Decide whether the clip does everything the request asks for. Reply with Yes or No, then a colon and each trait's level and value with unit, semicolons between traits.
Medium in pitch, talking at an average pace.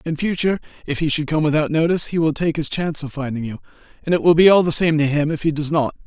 No: medium, 155 Hz; fast, 285 wpm